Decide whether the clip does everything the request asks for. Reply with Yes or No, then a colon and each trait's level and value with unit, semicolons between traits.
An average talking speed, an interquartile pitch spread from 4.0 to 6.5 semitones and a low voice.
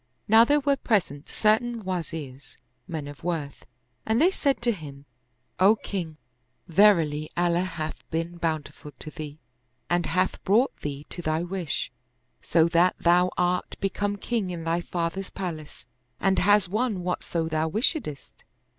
No: average, 145 wpm; average, 4.4 semitones; medium, 175 Hz